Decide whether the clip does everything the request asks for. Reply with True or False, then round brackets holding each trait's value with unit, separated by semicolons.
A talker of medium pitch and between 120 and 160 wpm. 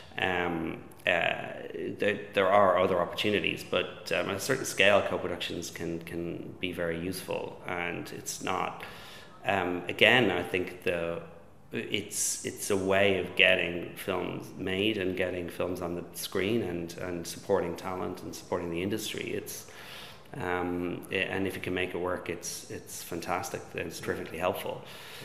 False (90 Hz; 155 wpm)